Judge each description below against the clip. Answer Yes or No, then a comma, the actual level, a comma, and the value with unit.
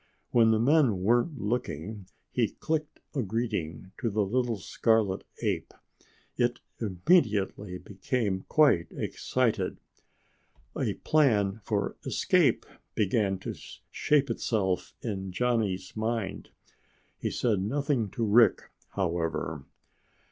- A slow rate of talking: Yes, slow, 105 wpm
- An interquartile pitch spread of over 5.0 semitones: No, average, 4.1 semitones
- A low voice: Yes, low, 110 Hz